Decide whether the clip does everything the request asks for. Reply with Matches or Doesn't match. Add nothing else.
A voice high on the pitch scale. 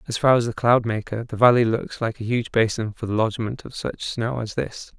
Doesn't match